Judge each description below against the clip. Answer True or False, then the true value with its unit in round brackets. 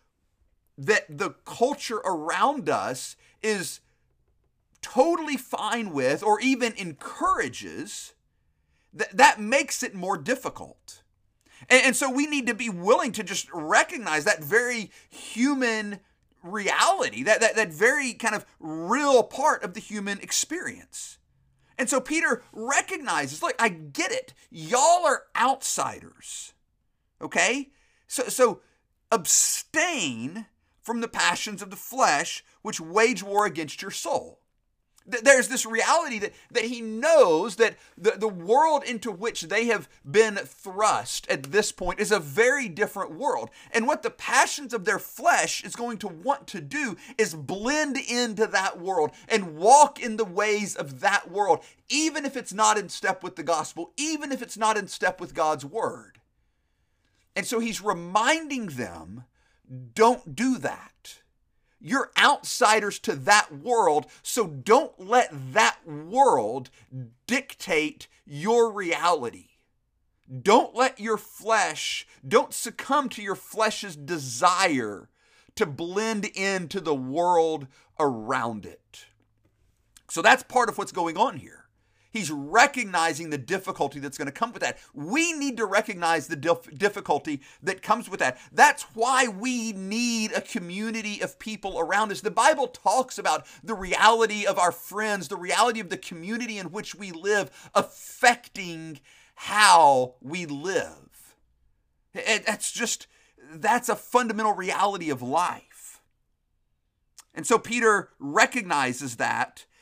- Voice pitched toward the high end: True (215 Hz)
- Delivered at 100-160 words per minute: True (140 wpm)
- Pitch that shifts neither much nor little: False (6.0 semitones)